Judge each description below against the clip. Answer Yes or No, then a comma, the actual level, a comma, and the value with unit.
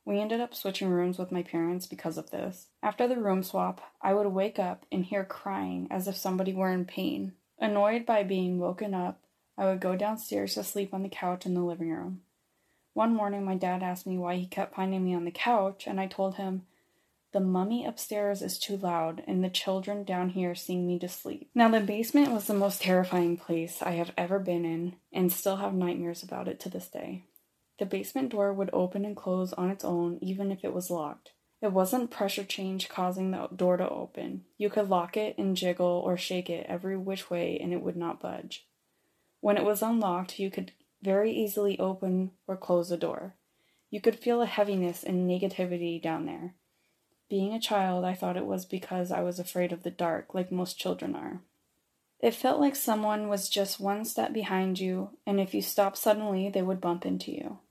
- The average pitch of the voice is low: No, high, 190 Hz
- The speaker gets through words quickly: Yes, fast, 210 wpm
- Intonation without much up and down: Yes, narrow, 2.1 semitones